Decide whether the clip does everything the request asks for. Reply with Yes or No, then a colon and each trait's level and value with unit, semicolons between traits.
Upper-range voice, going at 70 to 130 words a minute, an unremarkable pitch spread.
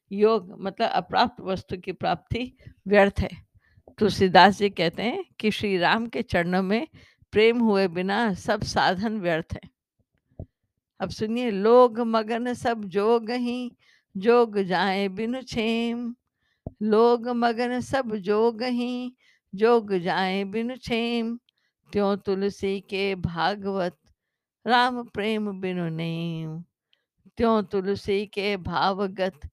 Yes: high, 210 Hz; slow, 110 wpm; average, 3.4 semitones